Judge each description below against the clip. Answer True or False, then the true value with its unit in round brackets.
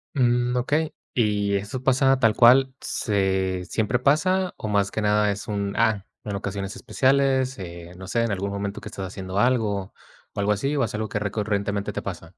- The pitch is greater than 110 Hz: False (105 Hz)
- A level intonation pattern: False (4.0 semitones)